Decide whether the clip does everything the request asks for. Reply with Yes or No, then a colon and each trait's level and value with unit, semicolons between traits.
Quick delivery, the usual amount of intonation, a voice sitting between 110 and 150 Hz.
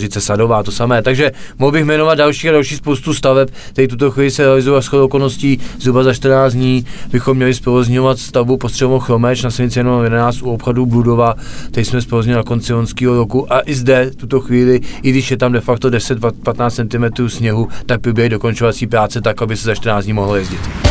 No: fast, 205 wpm; narrow, 2.2 semitones; low, 125 Hz